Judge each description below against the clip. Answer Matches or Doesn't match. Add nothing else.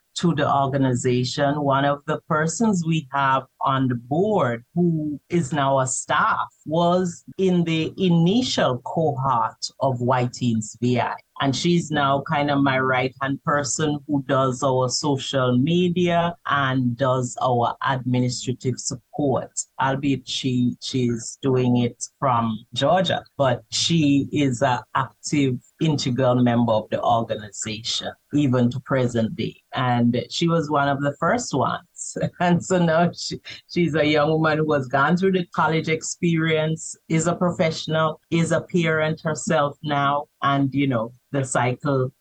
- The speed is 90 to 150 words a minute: Matches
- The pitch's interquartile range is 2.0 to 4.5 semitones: Matches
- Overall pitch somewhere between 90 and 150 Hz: Matches